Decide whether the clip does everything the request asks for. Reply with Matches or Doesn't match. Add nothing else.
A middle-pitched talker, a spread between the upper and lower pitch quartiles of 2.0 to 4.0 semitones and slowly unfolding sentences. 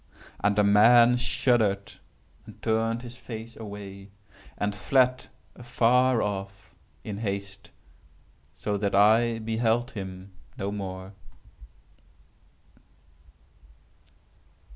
Doesn't match